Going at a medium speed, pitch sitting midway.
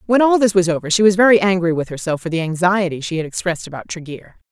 No: fast, 250 wpm; medium, 180 Hz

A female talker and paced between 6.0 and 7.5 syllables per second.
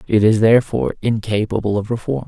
No: male; 6.4 syllables/s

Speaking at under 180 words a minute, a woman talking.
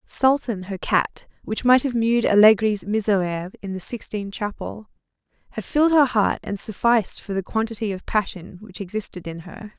Yes: average, 170 wpm; female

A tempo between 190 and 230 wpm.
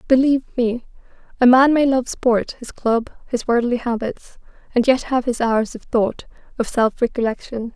No: average, 160 wpm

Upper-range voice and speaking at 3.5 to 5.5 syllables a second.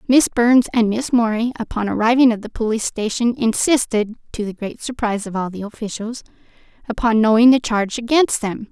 No: high, 230 Hz; 5.7 syllables/s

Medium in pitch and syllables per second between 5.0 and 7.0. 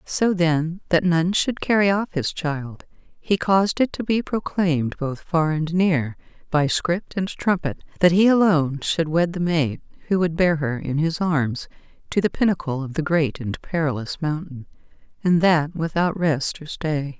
No: medium, 165 Hz; 4.4 syllables/s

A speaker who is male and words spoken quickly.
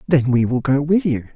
Yes: male; fast, 265 wpm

